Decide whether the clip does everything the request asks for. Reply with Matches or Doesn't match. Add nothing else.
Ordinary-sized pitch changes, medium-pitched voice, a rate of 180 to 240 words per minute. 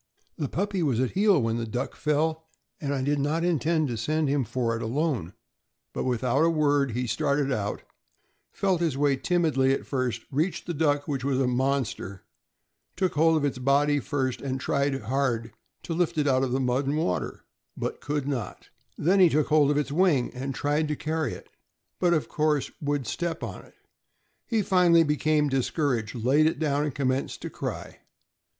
Matches